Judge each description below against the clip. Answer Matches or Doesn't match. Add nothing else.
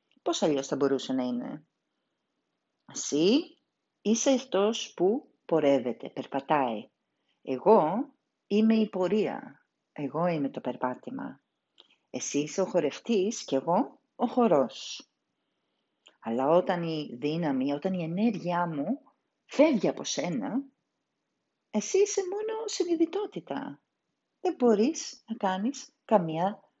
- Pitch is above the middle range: Matches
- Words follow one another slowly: Matches